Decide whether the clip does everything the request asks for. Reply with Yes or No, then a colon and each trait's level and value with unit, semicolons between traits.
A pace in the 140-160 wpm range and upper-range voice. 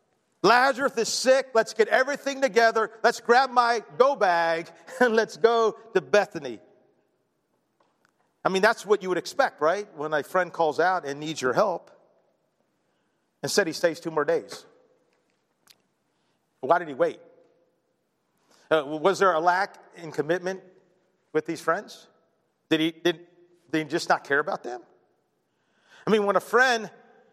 Yes: average, 155 wpm; high, 195 Hz